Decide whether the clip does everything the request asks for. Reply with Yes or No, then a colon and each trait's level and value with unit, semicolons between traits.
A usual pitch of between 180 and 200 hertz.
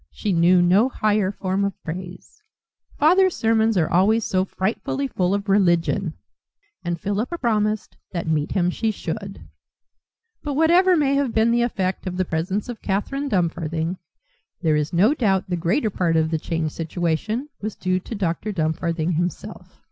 Yes: high, 190 Hz